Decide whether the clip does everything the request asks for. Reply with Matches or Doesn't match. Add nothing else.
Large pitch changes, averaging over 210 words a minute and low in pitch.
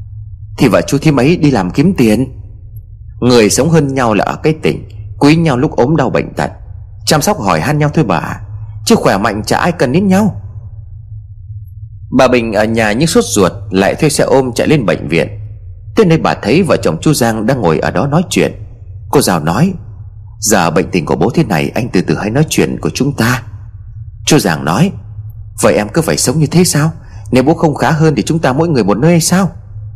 Matches